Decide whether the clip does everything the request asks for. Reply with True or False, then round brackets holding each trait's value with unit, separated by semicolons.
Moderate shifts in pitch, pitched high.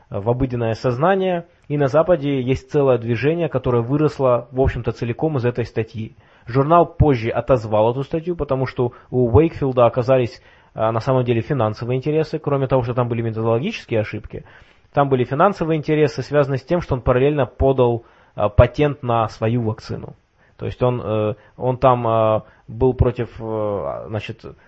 False (3.7 semitones; 125 Hz)